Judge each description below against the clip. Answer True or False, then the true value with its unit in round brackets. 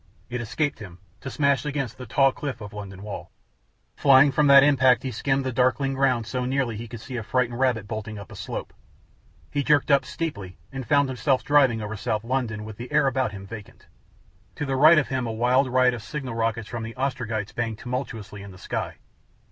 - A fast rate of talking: True (210 wpm)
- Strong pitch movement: False (3.7 semitones)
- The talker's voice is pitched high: False (125 Hz)